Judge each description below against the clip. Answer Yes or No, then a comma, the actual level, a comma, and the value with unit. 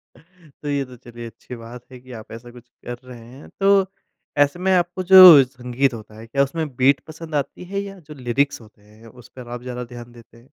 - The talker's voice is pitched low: Yes, low, 130 Hz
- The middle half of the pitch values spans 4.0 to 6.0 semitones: Yes, average, 4.5 semitones